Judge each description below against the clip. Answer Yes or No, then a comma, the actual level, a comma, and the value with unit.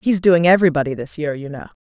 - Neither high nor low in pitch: Yes, medium, 160 Hz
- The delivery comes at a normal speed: No, fast, 230 wpm